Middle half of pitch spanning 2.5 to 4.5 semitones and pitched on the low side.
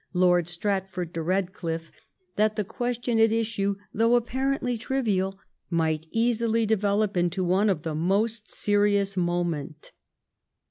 No: average, 4.2 semitones; high, 200 Hz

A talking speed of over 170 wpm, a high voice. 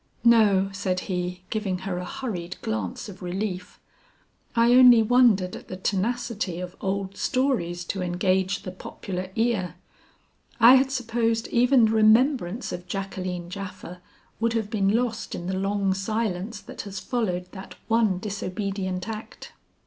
No: average, 145 wpm; high, 195 Hz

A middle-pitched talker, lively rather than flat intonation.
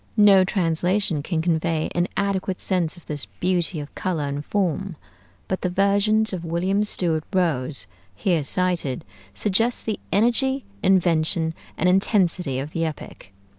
No: medium, 180 Hz; average, 3.5 semitones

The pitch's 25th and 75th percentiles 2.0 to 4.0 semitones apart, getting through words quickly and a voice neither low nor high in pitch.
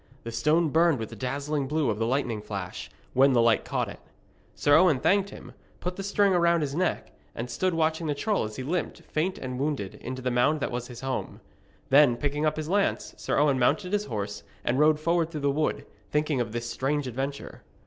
No: average, 4.6 semitones; fast, 220 wpm; medium, 145 Hz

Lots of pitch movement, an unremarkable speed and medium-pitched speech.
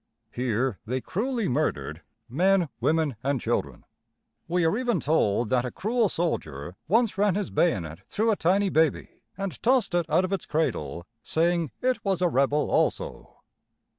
Yes: wide, 7.6 semitones; average, 160 wpm; medium, 165 Hz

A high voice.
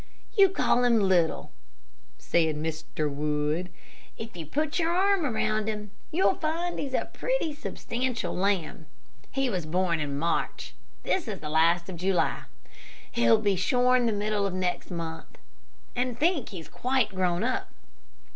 Yes: high, 200 Hz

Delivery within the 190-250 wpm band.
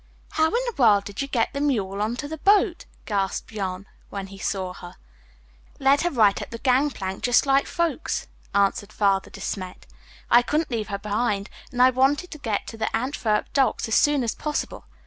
Yes: average, 200 wpm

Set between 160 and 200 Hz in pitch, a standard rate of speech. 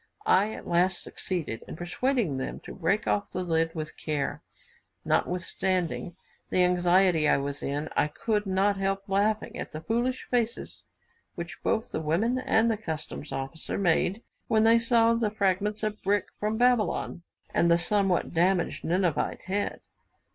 Yes: high, 190 Hz; average, 155 wpm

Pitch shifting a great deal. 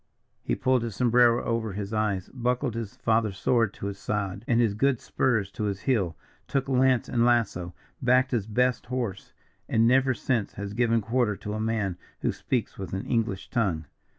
No: average, 3.5 semitones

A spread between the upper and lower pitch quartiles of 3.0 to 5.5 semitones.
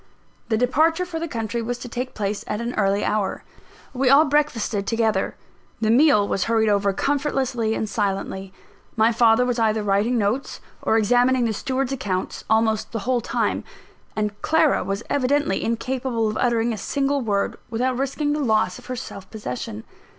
Yes: average, 3.5 semitones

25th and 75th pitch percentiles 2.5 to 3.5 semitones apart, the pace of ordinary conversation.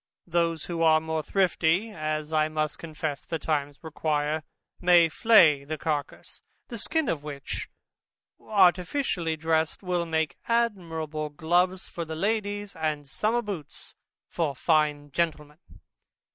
No: average, 2.8 semitones; slow, 125 wpm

